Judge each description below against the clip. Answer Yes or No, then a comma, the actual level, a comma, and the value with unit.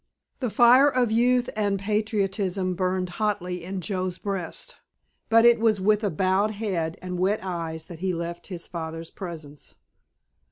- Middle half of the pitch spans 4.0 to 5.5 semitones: No, average, 3.4 semitones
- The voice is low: No, high, 190 Hz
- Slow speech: No, average, 150 wpm